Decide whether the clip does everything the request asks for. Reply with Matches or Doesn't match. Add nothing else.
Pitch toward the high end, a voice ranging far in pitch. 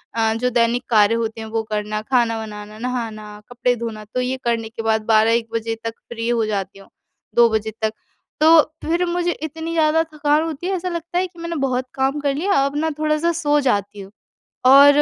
Matches